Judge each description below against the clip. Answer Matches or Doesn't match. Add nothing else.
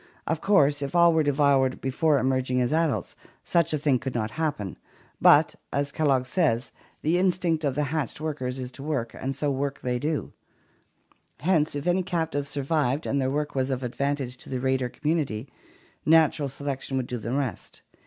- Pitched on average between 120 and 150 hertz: Matches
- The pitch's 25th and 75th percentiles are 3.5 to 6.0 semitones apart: Doesn't match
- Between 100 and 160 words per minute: Doesn't match